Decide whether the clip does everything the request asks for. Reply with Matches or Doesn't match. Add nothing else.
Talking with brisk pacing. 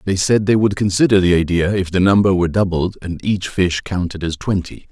Matches